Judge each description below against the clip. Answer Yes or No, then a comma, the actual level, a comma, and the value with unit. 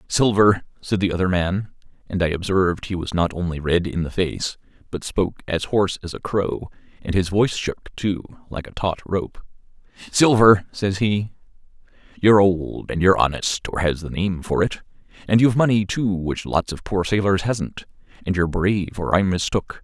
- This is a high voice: No, very low, 95 Hz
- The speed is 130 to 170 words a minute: No, average, 180 wpm